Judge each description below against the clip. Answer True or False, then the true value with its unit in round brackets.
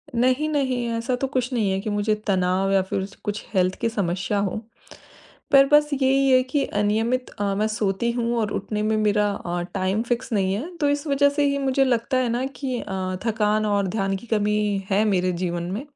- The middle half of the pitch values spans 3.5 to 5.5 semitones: True (4.7 semitones)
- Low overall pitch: False (215 Hz)